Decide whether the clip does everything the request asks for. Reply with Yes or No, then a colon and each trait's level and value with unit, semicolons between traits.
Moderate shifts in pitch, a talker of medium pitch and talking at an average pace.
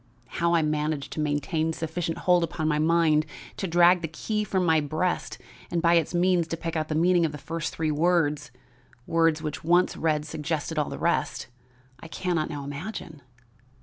No: narrow, 2.0 semitones; medium, 160 Hz; average, 190 wpm